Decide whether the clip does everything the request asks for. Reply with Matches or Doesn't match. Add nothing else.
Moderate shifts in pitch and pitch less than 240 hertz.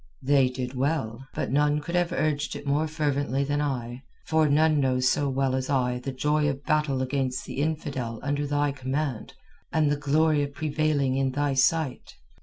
Doesn't match